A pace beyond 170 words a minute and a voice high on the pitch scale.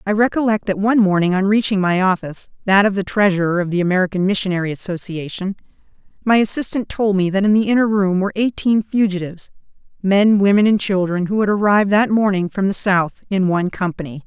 Yes: average, 190 wpm; high, 195 Hz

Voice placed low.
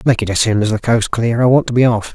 Yes: low, 115 Hz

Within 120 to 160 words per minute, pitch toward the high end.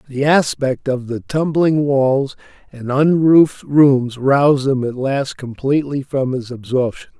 No: average, 140 wpm; low, 135 Hz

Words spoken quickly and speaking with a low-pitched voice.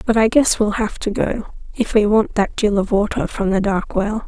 No: fast, 250 wpm; high, 210 Hz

